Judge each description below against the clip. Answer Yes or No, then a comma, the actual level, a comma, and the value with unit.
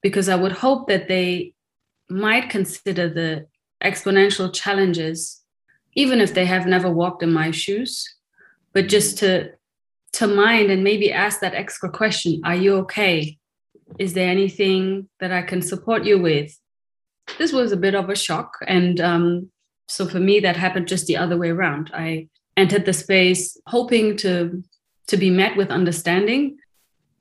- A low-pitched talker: No, high, 190 Hz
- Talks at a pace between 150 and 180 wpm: Yes, average, 160 wpm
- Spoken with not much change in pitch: Yes, narrow, 2.3 semitones